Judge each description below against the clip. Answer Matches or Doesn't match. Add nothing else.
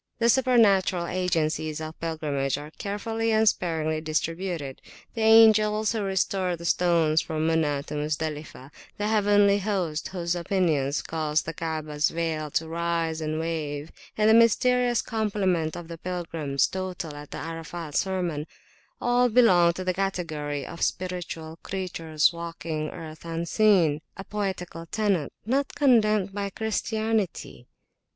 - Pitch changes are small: Doesn't match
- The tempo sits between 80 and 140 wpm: Matches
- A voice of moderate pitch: Matches